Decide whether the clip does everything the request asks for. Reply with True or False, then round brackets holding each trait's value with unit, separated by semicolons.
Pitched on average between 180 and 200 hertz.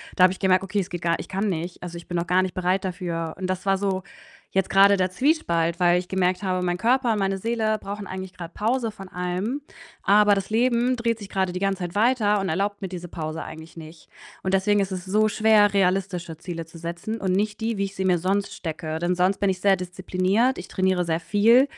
True (190 Hz)